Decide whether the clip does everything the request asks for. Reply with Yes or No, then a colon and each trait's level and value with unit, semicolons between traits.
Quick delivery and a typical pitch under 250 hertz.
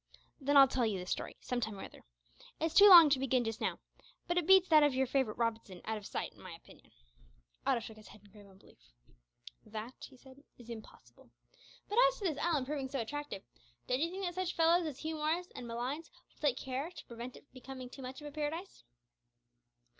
No: fast, 220 wpm; very high, 265 Hz